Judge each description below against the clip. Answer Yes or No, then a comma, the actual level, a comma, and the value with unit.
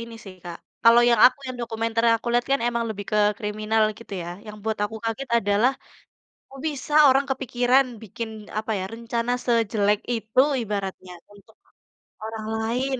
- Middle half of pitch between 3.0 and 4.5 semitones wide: No, narrow, 2.5 semitones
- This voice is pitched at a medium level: No, high, 230 Hz